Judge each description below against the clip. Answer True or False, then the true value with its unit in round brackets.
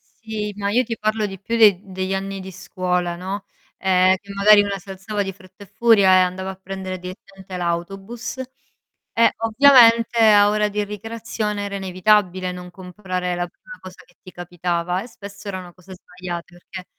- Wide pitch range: False (2.4 semitones)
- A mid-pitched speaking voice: False (195 Hz)